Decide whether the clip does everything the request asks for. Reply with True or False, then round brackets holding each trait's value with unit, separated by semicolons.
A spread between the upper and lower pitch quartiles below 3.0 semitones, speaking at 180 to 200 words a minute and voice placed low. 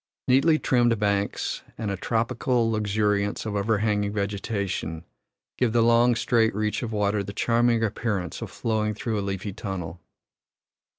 False (2.4 semitones; 140 wpm; 105 Hz)